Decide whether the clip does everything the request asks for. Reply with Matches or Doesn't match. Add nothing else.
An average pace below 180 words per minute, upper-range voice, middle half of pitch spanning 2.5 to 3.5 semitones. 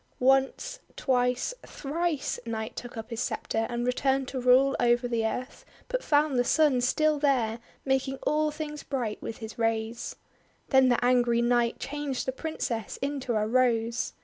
Matches